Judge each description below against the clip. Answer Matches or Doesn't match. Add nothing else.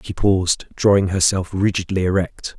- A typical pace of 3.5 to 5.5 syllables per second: Matches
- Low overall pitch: Matches